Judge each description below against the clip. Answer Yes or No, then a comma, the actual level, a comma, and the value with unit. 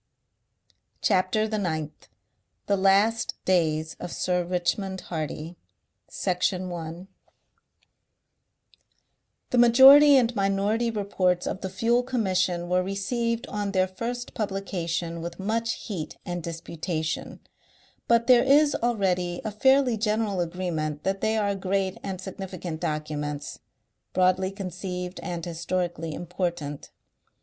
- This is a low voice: No, medium, 185 Hz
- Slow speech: Yes, slow, 115 wpm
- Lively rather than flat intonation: No, average, 3.7 semitones